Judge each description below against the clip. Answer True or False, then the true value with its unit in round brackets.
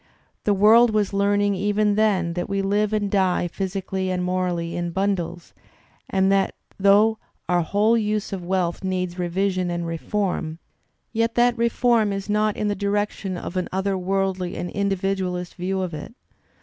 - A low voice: False (195 Hz)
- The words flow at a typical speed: True (165 wpm)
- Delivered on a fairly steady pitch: True (2.3 semitones)